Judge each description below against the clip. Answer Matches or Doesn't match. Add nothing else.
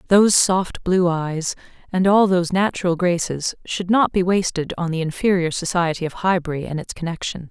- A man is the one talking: Doesn't match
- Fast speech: Doesn't match